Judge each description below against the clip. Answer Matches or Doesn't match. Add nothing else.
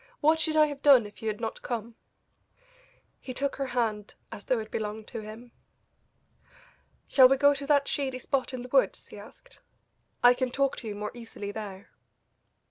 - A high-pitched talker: Matches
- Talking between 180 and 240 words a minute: Matches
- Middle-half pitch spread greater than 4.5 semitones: Doesn't match